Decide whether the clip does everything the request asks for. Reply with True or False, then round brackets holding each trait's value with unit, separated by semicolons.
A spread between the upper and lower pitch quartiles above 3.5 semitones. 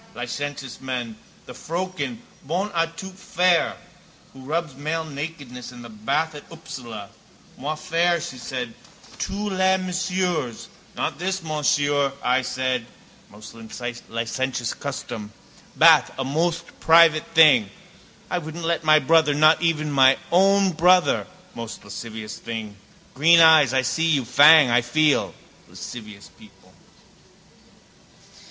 True (5.0 semitones)